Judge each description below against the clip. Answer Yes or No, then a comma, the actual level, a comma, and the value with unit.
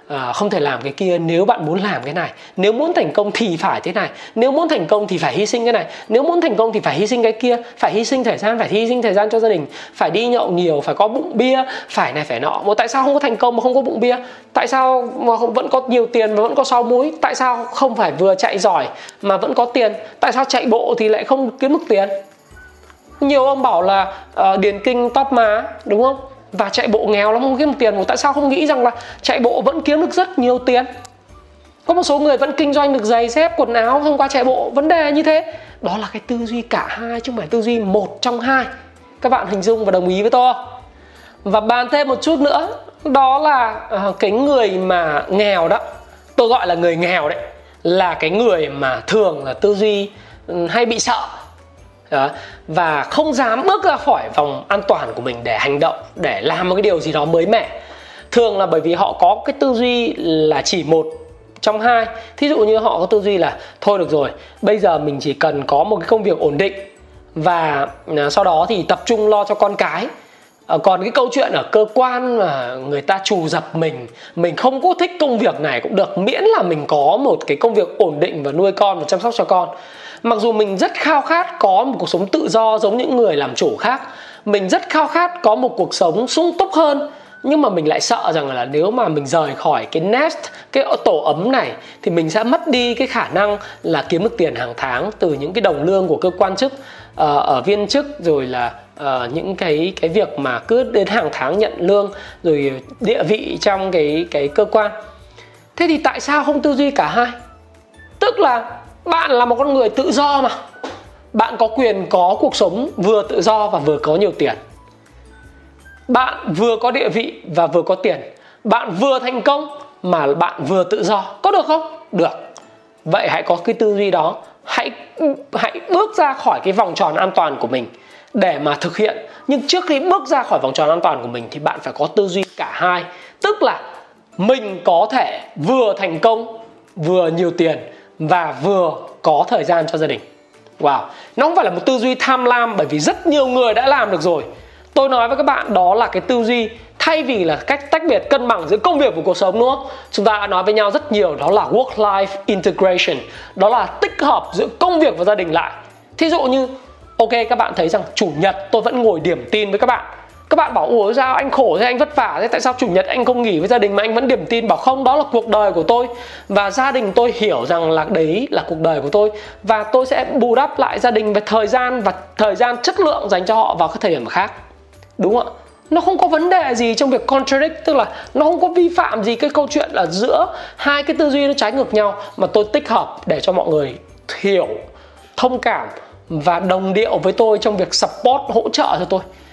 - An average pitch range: No, wide, 5.7 semitones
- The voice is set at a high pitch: Yes, high, 230 Hz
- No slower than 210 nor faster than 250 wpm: Yes, average, 240 wpm